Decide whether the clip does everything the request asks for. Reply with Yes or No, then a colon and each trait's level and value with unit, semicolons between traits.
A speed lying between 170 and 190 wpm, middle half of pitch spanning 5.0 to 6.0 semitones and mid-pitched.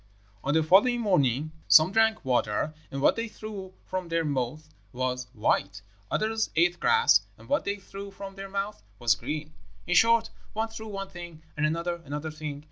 Yes: average, 180 wpm; wide, 5.4 semitones; medium, 175 Hz